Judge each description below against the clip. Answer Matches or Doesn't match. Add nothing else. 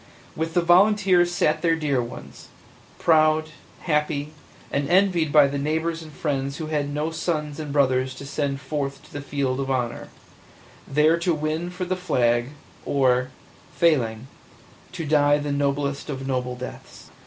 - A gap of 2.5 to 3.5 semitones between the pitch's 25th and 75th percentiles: Matches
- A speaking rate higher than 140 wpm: Matches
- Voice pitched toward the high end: Doesn't match